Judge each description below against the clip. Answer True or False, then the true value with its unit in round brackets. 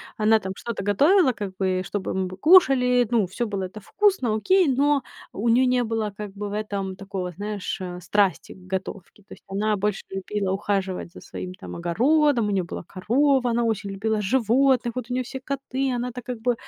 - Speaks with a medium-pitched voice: False (215 Hz)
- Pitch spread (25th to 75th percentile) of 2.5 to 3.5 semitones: False (4.5 semitones)